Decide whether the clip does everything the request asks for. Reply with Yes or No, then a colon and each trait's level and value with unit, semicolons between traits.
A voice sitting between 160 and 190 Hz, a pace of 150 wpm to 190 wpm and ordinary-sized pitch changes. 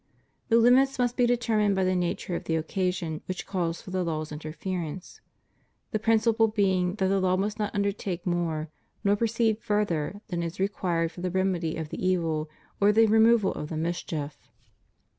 Yes: medium, 185 Hz; average, 180 wpm; average, 4.0 semitones